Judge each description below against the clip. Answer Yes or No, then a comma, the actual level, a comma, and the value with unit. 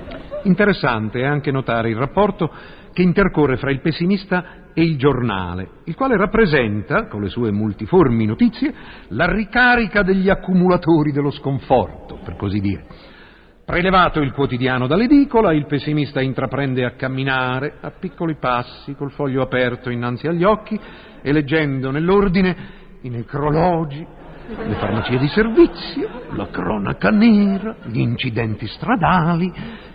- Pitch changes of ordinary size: No, wide, 6.8 semitones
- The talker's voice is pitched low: No, medium, 150 Hz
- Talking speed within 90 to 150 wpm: Yes, average, 130 wpm